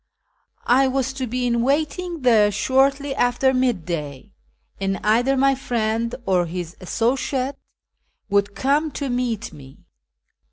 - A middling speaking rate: No, slow, 130 wpm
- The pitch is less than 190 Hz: No, high, 245 Hz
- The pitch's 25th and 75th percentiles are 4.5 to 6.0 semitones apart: Yes, average, 4.9 semitones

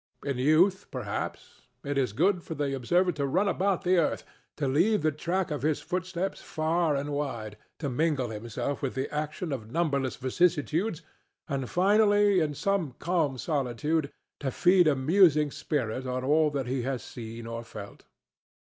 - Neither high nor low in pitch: Yes, medium, 150 Hz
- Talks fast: No, average, 165 wpm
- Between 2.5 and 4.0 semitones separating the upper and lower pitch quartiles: No, average, 4.9 semitones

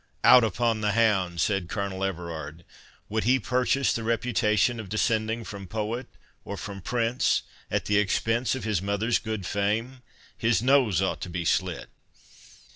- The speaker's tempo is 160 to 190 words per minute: No, average, 150 wpm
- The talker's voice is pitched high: No, low, 110 Hz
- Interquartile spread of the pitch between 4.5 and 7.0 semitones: No, average, 3.2 semitones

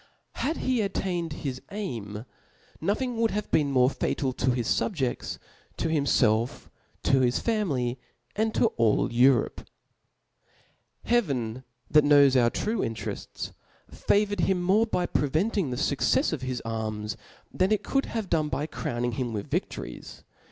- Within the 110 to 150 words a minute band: Yes, average, 145 wpm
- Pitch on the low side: No, medium, 145 Hz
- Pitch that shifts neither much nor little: No, wide, 8.6 semitones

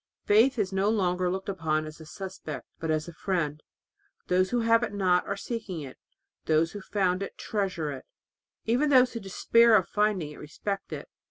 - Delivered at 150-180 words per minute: No, average, 200 wpm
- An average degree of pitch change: Yes, average, 4.3 semitones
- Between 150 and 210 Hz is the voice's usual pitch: Yes, high, 190 Hz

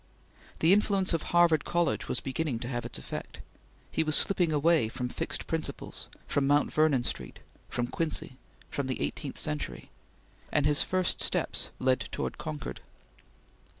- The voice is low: No, medium, 145 Hz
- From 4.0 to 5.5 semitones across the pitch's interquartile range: Yes, average, 4.6 semitones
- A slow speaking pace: No, average, 150 wpm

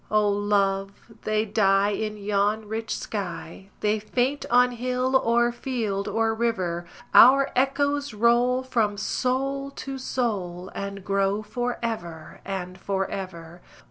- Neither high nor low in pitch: No, high, 215 Hz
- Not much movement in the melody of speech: No, average, 4.0 semitones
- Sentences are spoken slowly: Yes, slow, 130 wpm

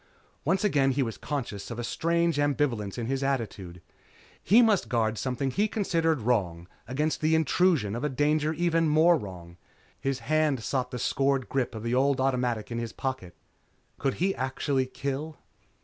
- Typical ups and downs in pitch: Yes, average, 4.9 semitones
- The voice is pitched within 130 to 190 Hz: Yes, low, 135 Hz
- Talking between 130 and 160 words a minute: No, average, 170 wpm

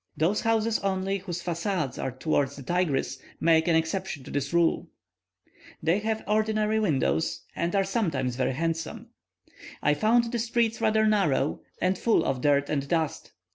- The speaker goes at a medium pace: Yes, average, 160 wpm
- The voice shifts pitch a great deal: Yes, wide, 6.5 semitones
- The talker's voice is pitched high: No, medium, 175 Hz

